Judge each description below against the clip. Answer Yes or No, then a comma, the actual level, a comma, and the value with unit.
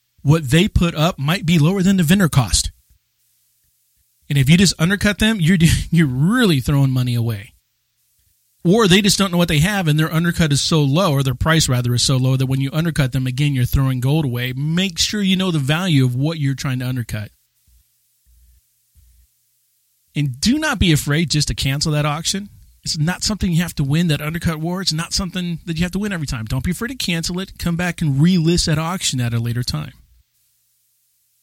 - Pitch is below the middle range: No, medium, 155 Hz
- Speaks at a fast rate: Yes, fast, 215 wpm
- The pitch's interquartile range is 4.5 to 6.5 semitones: Yes, average, 5.1 semitones